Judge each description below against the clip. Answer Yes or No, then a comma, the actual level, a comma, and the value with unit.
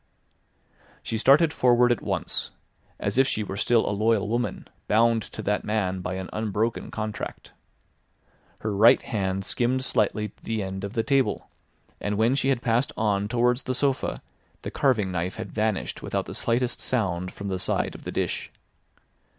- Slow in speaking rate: No, average, 170 wpm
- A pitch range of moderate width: Yes, average, 3.3 semitones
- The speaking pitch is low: Yes, low, 110 Hz